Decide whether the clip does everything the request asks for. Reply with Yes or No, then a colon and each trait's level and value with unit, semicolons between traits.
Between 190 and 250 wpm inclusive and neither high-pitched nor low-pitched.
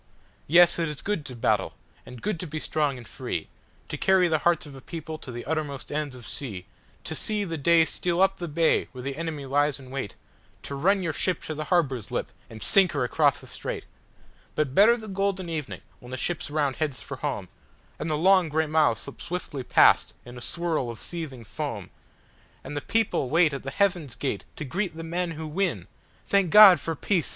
Yes: average, 200 wpm; medium, 155 Hz